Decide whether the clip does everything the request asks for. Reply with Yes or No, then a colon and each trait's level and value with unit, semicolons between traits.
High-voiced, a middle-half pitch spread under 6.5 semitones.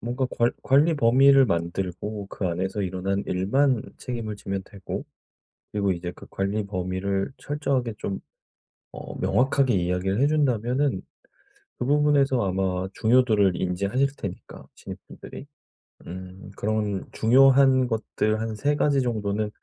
No: low, 110 Hz; wide, 5.5 semitones